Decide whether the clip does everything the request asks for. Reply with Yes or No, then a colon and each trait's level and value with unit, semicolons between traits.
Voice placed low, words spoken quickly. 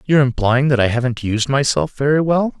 Yes: low, 130 Hz; fast, 210 wpm